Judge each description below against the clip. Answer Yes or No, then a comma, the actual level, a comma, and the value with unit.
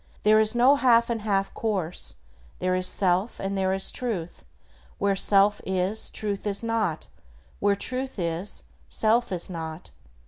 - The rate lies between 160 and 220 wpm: No, average, 150 wpm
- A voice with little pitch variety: No, average, 3.2 semitones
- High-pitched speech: Yes, high, 200 Hz